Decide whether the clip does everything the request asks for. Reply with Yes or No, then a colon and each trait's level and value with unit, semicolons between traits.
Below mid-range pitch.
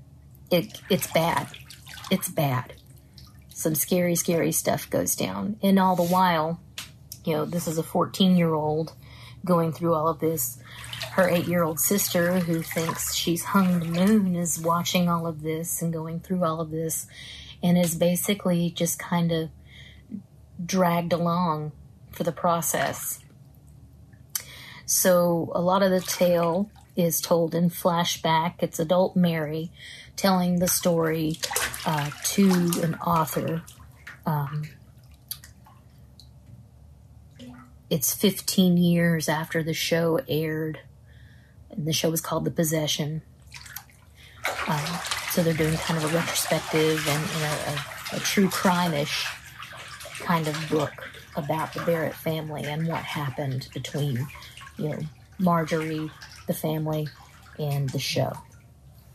No: medium, 165 Hz